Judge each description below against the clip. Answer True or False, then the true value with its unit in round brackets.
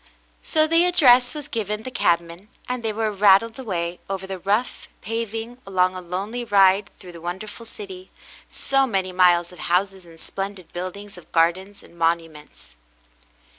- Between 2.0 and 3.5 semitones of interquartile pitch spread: False (4.0 semitones)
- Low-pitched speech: False (195 Hz)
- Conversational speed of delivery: True (165 wpm)